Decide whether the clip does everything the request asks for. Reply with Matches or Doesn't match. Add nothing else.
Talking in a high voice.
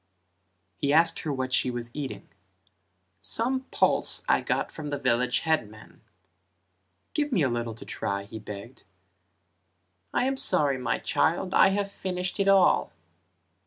Doesn't match